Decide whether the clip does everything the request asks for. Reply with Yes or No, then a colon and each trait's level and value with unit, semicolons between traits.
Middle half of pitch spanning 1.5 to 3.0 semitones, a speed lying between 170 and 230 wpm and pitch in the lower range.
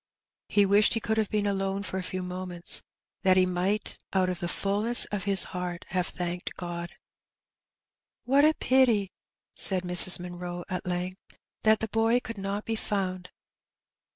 No: average, 2.7 semitones; average, 175 wpm; high, 190 Hz